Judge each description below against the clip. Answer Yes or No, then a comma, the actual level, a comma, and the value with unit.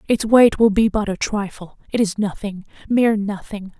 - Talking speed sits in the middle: Yes, average, 160 wpm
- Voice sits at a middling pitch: No, high, 205 Hz